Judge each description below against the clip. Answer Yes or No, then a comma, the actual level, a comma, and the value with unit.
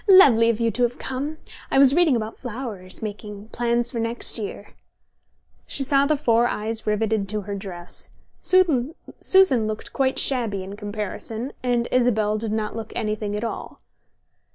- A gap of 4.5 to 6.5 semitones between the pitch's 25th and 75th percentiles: No, average, 3.2 semitones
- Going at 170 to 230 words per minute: No, average, 160 wpm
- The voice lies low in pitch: No, high, 230 Hz